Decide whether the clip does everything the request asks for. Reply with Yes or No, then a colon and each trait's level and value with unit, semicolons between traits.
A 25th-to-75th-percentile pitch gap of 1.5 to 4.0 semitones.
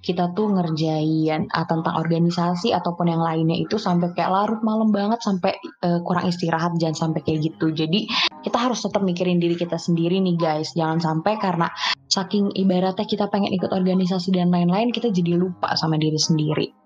Yes: average, 3.2 semitones